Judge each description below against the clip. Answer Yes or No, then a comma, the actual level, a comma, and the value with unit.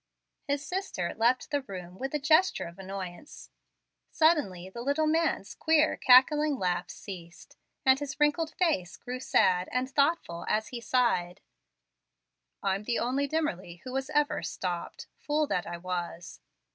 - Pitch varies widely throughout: Yes, wide, 8.4 semitones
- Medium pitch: No, very high, 250 Hz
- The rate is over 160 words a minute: No, average, 145 wpm